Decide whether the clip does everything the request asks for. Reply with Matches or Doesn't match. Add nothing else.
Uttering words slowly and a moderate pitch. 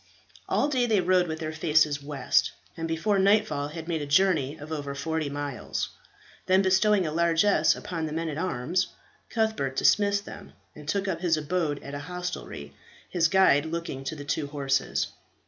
Doesn't match